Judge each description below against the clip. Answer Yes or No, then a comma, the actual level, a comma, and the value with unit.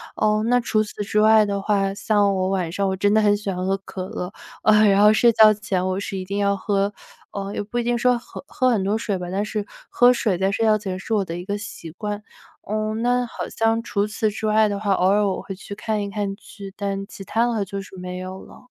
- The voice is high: Yes, high, 205 Hz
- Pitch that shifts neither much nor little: No, narrow, 1.8 semitones